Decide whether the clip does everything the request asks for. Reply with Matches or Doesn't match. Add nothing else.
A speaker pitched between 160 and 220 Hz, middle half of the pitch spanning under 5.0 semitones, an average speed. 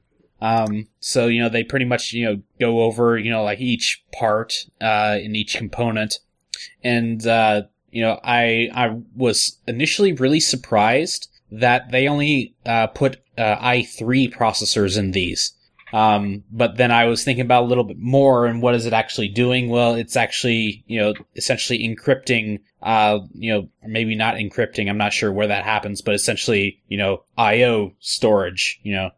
Doesn't match